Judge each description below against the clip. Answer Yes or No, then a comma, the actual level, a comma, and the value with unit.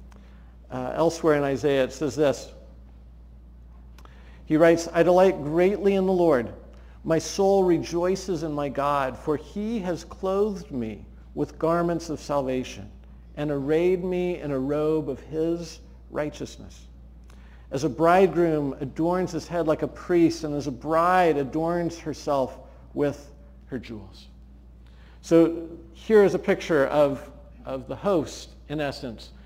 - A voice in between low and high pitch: Yes, medium, 145 Hz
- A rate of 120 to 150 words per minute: Yes, average, 140 wpm